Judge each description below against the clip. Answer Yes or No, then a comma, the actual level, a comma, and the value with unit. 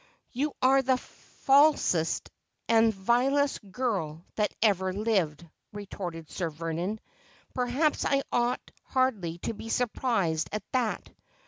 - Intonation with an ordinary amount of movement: No, wide, 6.3 semitones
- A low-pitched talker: No, high, 220 Hz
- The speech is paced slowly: Yes, slow, 125 wpm